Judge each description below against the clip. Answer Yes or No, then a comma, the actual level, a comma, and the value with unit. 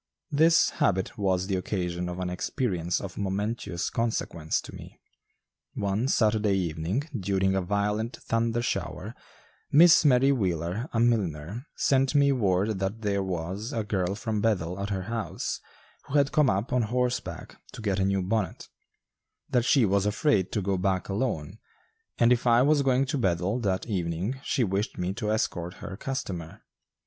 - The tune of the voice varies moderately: Yes, average, 4.3 semitones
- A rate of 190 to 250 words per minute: No, average, 165 wpm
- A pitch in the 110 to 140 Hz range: No, low, 100 Hz